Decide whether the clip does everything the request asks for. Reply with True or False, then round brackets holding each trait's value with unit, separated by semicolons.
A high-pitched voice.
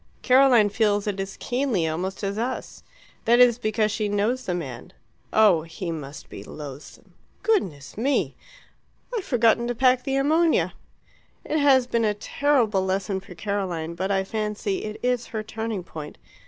True (215 Hz)